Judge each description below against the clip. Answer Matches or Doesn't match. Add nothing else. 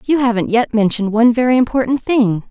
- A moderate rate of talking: Matches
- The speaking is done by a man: Doesn't match